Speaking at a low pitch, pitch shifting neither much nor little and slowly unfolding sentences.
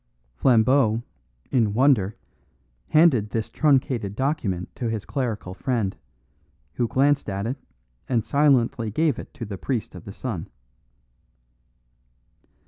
Yes: low, 115 Hz; average, 4.5 semitones; slow, 120 wpm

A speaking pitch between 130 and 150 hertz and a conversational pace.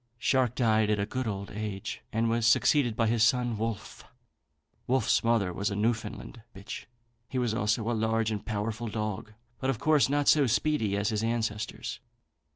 No: low, 115 Hz; average, 175 wpm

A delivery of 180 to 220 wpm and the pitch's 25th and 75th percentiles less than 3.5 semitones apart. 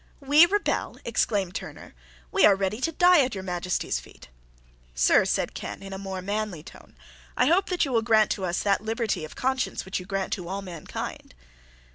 No: average, 195 wpm; average, 5.3 semitones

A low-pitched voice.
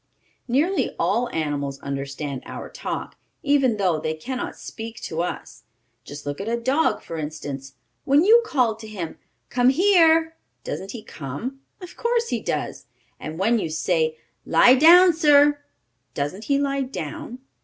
No: high, 230 Hz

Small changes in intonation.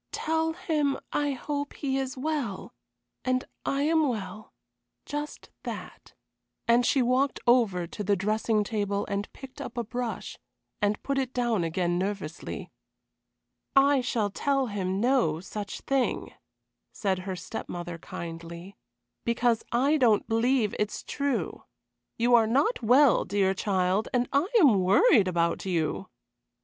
No: wide, 5.6 semitones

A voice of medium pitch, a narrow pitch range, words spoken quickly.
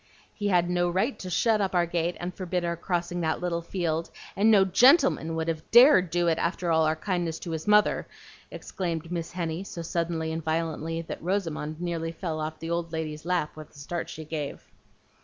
Yes: medium, 170 Hz; narrow, 2.0 semitones; fast, 210 wpm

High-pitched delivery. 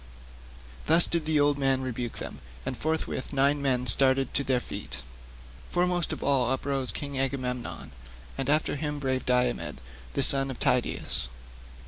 No: low, 135 Hz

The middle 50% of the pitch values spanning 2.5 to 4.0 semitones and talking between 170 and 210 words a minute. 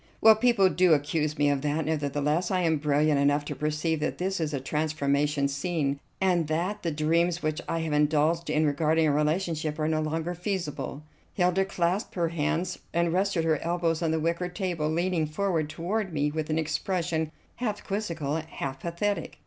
Yes: average, 2.8 semitones; average, 180 wpm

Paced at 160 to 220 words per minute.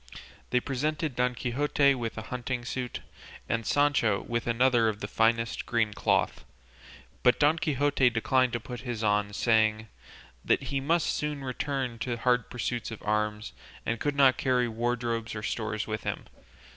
Yes: average, 165 wpm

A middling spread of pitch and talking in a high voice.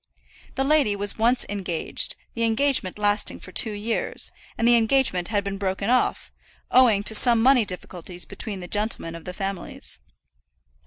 Yes: average, 3.4 semitones; high, 210 Hz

